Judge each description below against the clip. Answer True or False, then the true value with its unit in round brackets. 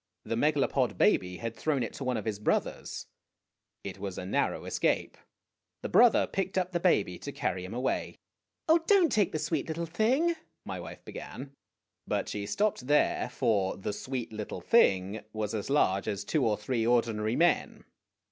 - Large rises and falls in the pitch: True (7.9 semitones)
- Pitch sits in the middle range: False (120 Hz)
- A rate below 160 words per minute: False (175 wpm)